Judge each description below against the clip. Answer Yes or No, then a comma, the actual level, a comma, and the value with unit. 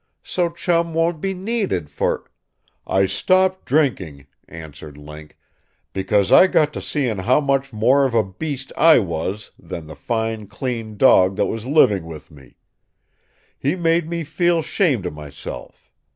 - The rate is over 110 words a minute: Yes, average, 155 wpm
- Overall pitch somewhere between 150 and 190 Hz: No, low, 120 Hz